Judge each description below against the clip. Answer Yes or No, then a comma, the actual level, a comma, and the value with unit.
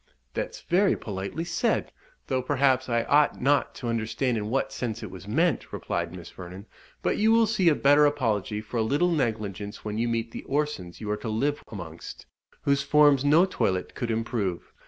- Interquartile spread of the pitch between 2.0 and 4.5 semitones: No, wide, 5.6 semitones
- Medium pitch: No, low, 120 Hz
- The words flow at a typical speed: Yes, average, 190 wpm